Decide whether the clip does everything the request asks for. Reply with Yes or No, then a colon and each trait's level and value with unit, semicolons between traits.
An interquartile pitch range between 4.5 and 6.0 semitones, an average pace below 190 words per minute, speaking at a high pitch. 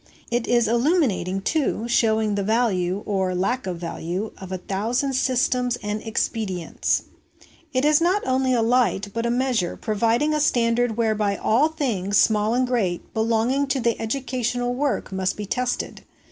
No: average, 3.9 semitones; average, 155 wpm; high, 230 Hz